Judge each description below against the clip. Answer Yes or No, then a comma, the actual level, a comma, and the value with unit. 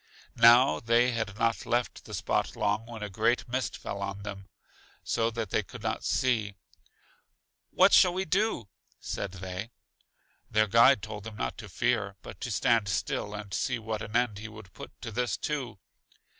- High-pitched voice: No, low, 110 Hz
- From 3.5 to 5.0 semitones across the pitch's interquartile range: No, average, 2.7 semitones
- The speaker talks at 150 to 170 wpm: No, average, 180 wpm